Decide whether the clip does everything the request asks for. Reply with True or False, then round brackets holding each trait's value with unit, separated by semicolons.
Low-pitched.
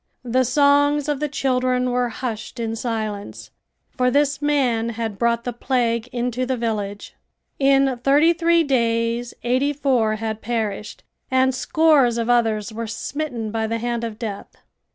False (245 Hz)